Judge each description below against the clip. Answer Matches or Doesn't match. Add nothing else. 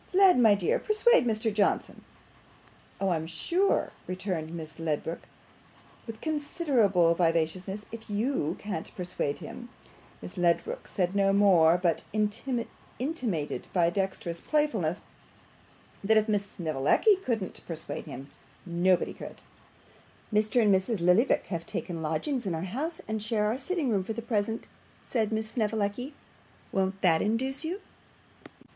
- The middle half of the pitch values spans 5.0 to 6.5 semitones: Matches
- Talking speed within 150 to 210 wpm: Doesn't match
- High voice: Matches